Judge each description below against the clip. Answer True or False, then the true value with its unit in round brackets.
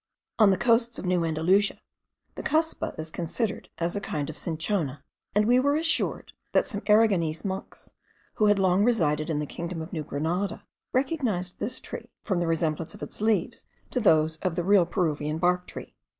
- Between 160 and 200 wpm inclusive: True (185 wpm)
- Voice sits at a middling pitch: True (180 Hz)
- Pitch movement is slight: False (4.9 semitones)